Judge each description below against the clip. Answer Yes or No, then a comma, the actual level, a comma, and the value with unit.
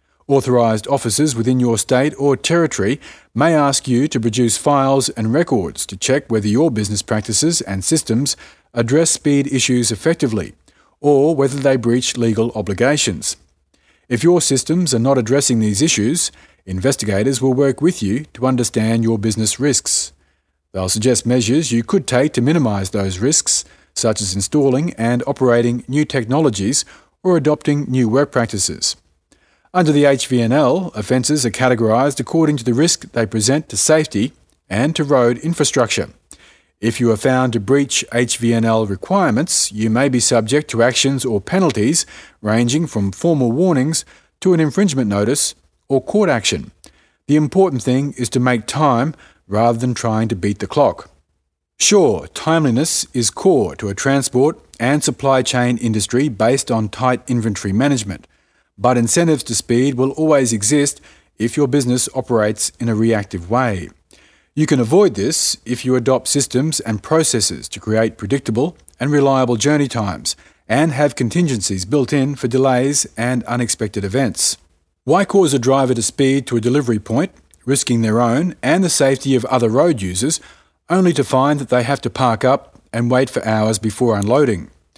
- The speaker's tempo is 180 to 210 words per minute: No, average, 160 wpm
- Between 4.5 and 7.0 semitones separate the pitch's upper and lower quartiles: No, average, 3.9 semitones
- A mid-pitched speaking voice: No, low, 125 Hz